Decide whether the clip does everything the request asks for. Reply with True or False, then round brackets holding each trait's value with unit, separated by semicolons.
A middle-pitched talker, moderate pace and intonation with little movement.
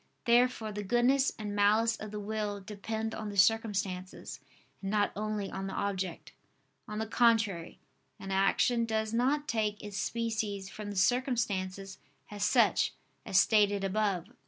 False (210 Hz; 155 wpm; 2.2 semitones)